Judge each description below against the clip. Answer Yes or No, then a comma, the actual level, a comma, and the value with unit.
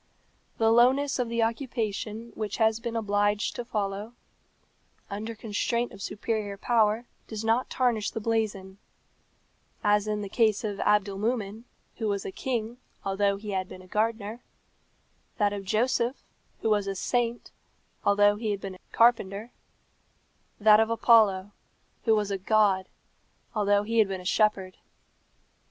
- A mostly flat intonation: Yes, narrow, 2.2 semitones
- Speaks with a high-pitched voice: Yes, high, 215 Hz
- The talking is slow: No, average, 150 wpm